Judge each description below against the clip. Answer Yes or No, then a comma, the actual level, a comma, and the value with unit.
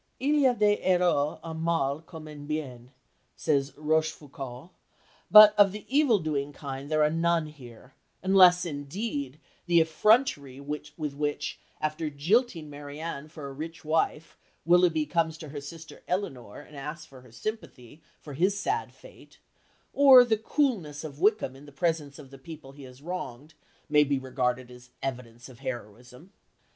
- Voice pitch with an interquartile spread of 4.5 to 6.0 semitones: No, average, 3.9 semitones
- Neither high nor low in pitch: Yes, medium, 150 Hz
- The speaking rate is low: No, average, 160 wpm